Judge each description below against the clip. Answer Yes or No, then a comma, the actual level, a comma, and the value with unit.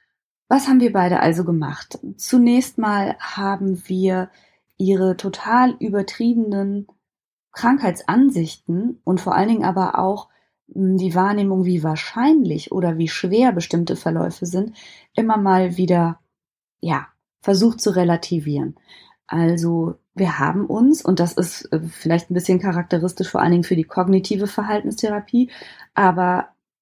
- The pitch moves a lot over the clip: No, average, 3.4 semitones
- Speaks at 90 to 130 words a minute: Yes, slow, 125 wpm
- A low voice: No, medium, 185 Hz